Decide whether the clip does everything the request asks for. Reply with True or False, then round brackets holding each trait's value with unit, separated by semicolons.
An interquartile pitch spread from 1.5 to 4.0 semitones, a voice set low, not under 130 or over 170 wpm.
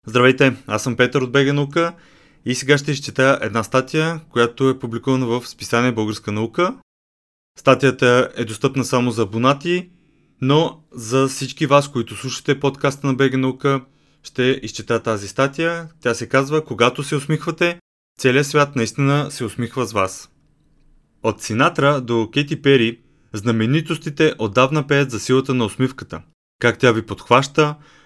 True (3.6 semitones; 130 Hz; 150 wpm)